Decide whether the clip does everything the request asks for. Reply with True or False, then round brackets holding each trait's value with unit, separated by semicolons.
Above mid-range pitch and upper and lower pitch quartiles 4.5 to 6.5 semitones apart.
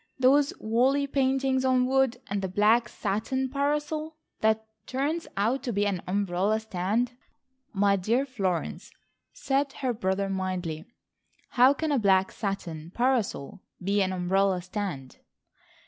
True (220 Hz; 5.5 semitones)